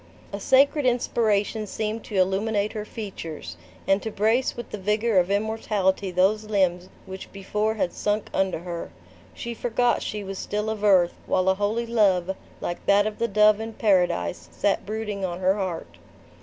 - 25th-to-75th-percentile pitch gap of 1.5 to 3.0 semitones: Yes, narrow, 2.6 semitones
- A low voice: No, high, 205 Hz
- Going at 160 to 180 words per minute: Yes, average, 170 wpm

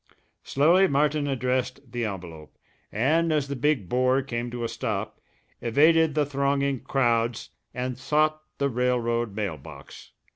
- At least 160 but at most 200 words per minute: No, average, 140 wpm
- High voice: No, low, 130 Hz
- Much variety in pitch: No, average, 3.4 semitones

